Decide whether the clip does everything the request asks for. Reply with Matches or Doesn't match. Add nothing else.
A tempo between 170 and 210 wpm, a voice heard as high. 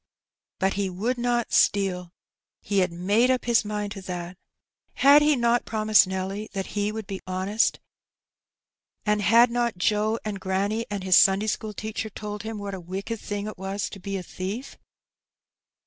Matches